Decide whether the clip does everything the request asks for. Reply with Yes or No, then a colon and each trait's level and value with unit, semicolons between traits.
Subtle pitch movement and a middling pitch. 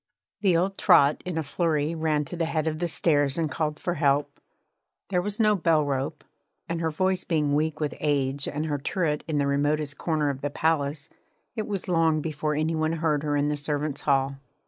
Yes: narrow, 2.2 semitones; medium, 155 Hz